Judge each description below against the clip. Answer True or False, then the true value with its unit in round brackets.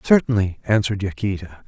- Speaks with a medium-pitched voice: False (105 Hz)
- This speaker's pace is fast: False (110 wpm)